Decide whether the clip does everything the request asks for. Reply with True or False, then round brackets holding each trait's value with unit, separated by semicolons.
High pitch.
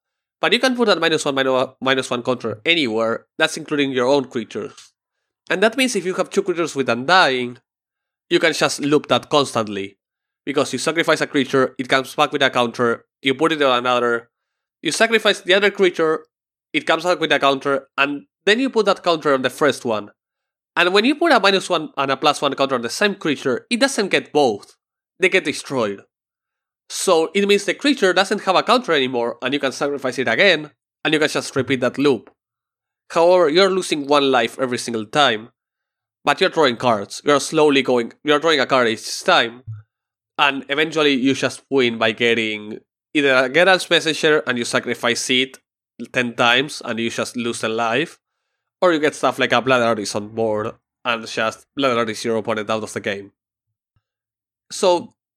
False (140 Hz)